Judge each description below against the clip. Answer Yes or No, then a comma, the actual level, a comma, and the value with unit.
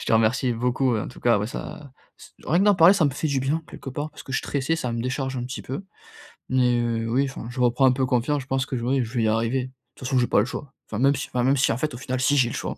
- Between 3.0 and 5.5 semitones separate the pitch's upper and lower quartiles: No, narrow, 2.4 semitones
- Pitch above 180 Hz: No, low, 130 Hz